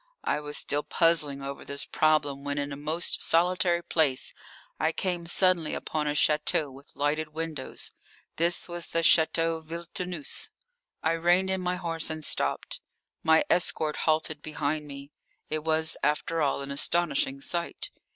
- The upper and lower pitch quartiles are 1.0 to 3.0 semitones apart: Yes, narrow, 2.4 semitones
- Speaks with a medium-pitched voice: Yes, medium, 155 Hz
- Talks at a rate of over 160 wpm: No, average, 150 wpm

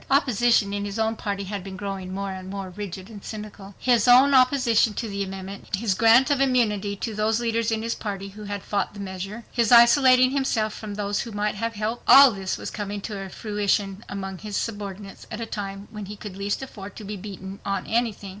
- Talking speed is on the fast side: Yes, fast, 210 wpm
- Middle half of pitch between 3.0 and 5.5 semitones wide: No, narrow, 2.6 semitones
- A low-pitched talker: No, high, 210 Hz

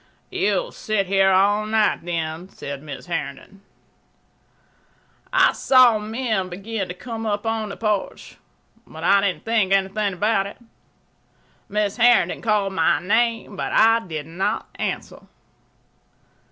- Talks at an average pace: No, slow, 125 wpm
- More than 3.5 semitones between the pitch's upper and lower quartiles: No, average, 3.2 semitones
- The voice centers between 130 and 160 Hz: No, high, 200 Hz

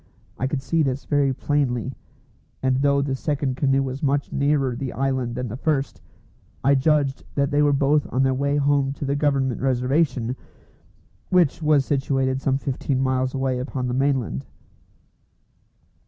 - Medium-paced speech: Yes, average, 160 wpm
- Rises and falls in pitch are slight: Yes, narrow, 1.5 semitones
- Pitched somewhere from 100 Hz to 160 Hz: Yes, low, 135 Hz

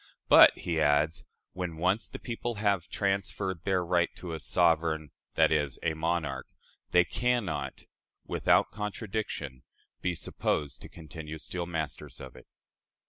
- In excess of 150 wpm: No, average, 140 wpm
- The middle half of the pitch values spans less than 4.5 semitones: Yes, average, 3.5 semitones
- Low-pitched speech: Yes, very low, 85 Hz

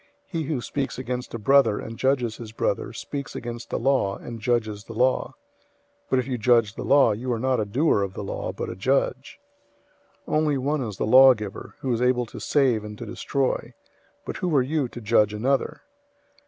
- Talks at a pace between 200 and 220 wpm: Yes, fast, 205 wpm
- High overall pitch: No, low, 125 Hz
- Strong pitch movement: No, average, 3.5 semitones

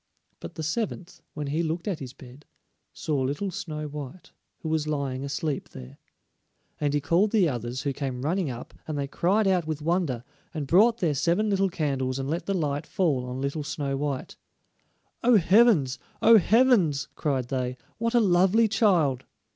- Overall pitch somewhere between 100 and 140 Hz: No, medium, 155 Hz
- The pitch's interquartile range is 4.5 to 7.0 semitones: Yes, wide, 5.4 semitones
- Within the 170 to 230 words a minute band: Yes, average, 180 wpm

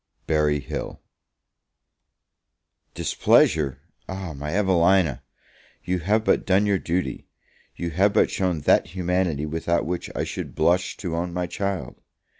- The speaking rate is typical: No, slow, 125 wpm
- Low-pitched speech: Yes, very low, 90 Hz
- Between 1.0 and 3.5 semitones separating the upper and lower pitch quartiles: Yes, average, 3.0 semitones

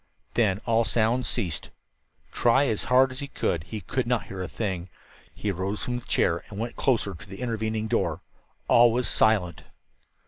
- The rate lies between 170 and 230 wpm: Yes, average, 180 wpm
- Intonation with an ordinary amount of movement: Yes, average, 3.8 semitones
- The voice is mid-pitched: No, low, 110 Hz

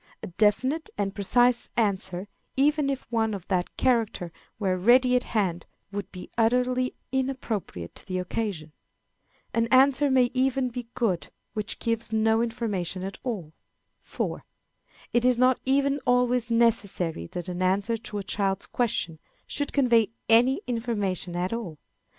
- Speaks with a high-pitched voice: Yes, high, 230 Hz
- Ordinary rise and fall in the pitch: Yes, average, 4.6 semitones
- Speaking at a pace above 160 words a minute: No, average, 145 wpm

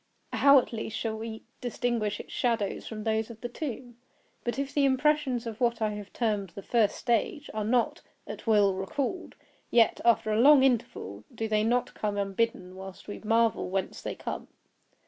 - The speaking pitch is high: Yes, high, 225 Hz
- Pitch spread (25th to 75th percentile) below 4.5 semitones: Yes, average, 2.8 semitones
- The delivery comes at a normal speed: Yes, average, 180 wpm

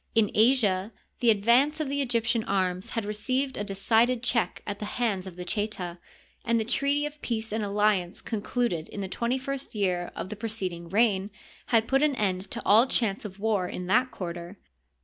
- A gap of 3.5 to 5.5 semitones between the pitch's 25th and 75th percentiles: Yes, average, 3.9 semitones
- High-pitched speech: Yes, high, 215 Hz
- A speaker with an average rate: Yes, average, 190 wpm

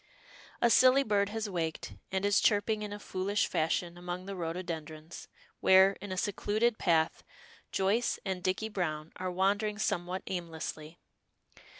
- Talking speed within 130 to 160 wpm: Yes, average, 140 wpm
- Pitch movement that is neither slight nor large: Yes, average, 3.0 semitones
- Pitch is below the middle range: No, high, 190 Hz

